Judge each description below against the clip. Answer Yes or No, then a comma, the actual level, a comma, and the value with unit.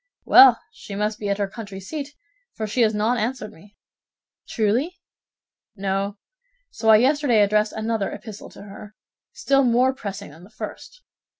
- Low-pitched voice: No, high, 215 Hz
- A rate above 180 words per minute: No, average, 160 wpm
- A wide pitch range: No, average, 3.4 semitones